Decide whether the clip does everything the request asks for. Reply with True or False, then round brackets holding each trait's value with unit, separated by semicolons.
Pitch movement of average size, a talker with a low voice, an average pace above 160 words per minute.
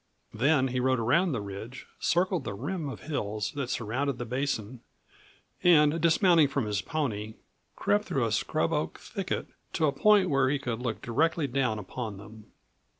False (5.9 semitones; 130 Hz; 170 wpm)